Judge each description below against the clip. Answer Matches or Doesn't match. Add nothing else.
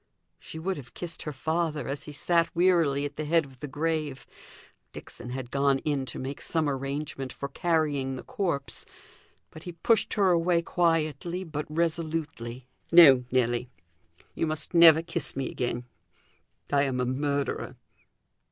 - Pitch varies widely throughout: Doesn't match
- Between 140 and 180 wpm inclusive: Matches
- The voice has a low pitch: Doesn't match